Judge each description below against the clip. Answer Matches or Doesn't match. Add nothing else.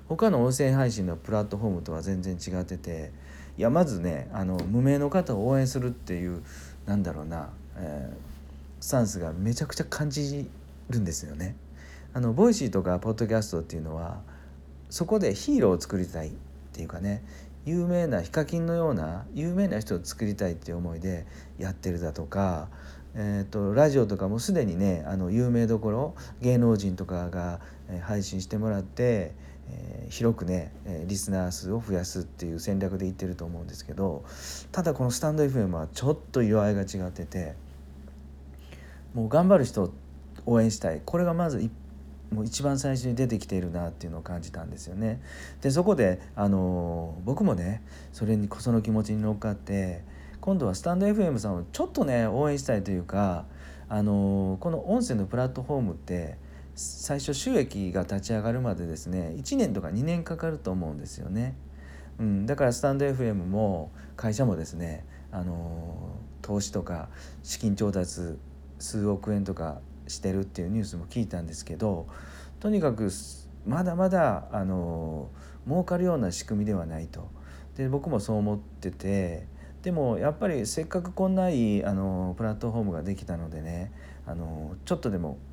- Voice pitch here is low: Matches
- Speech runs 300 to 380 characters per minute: Matches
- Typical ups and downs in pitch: Doesn't match